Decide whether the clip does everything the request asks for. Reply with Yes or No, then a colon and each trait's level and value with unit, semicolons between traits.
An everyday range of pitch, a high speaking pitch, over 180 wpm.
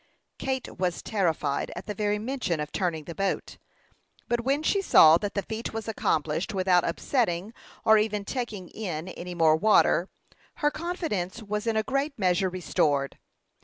No: average, 4.6 semitones; high, 200 Hz; average, 165 wpm